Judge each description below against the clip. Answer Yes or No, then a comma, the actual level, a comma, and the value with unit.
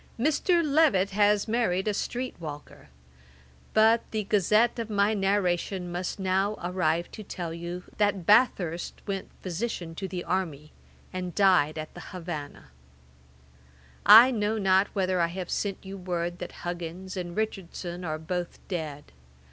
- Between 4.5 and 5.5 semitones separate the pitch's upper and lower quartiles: No, average, 3.2 semitones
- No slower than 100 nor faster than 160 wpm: Yes, average, 150 wpm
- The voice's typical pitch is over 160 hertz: Yes, medium, 185 Hz